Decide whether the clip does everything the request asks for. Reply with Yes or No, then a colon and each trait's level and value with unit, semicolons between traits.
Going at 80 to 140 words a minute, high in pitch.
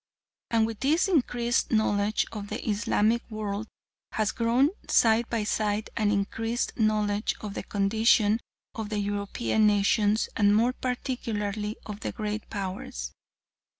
Yes: slow, 135 wpm; high, 215 Hz